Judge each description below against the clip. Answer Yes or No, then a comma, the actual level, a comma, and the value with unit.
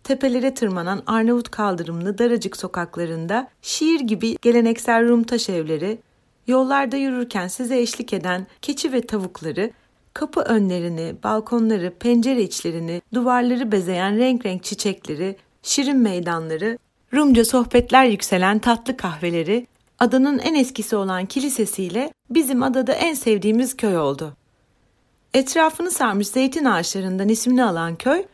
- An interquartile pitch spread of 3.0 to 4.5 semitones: No, average, 5.3 semitones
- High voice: Yes, high, 230 Hz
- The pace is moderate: Yes, average, 115 wpm